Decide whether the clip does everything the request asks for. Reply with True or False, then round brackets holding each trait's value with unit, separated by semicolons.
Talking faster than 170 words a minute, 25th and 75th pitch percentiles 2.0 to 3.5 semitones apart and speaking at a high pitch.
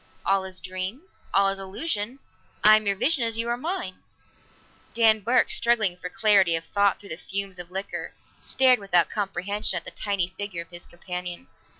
True (185 wpm; 3.0 semitones; 200 Hz)